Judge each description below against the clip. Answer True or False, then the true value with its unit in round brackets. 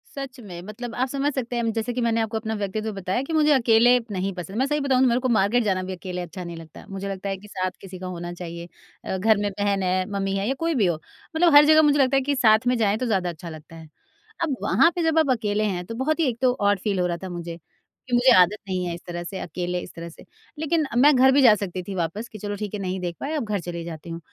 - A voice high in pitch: True (205 Hz)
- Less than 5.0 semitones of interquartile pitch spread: False (5.5 semitones)